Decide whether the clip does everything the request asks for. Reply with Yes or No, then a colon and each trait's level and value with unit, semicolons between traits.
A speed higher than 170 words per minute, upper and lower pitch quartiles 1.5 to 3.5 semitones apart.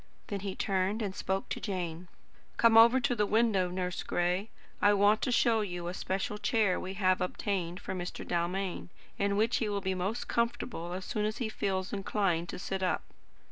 Yes: average, 195 wpm; narrow, 2.6 semitones